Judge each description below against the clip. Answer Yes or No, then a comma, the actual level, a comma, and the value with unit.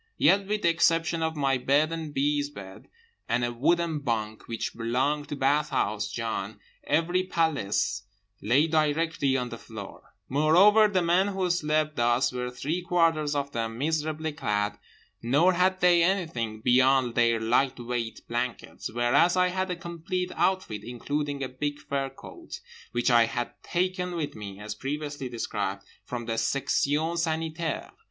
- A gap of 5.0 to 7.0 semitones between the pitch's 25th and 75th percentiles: Yes, wide, 5.6 semitones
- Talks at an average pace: Yes, average, 150 wpm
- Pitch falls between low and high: Yes, medium, 145 Hz